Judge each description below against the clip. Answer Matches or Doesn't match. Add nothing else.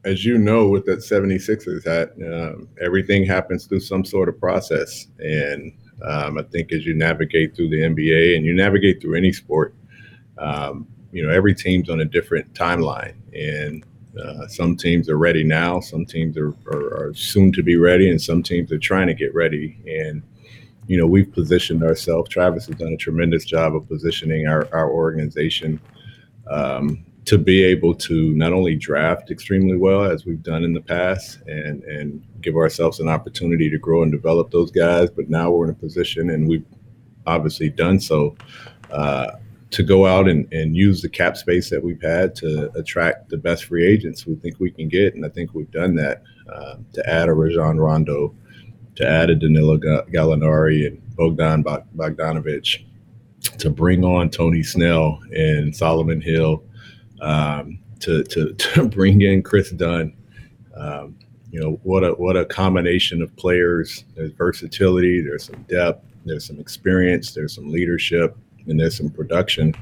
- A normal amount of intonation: Matches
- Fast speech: Doesn't match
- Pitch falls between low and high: Doesn't match